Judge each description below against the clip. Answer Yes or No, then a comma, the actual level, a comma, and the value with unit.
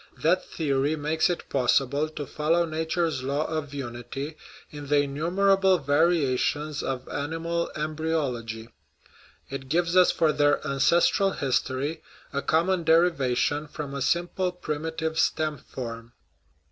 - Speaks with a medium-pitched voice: Yes, medium, 150 Hz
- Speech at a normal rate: No, slow, 120 wpm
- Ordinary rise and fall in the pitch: Yes, average, 3.1 semitones